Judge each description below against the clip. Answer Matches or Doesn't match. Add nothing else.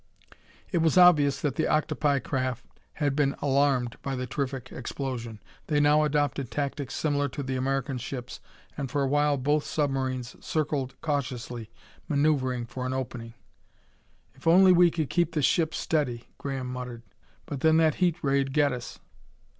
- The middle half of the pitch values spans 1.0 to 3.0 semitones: Matches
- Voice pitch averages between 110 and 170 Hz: Matches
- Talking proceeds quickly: Doesn't match